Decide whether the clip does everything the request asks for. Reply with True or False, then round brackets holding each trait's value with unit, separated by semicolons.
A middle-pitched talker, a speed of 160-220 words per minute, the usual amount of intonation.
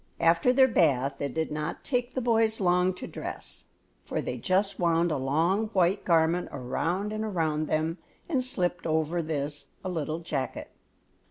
True (170 Hz; 165 wpm; 4.2 semitones)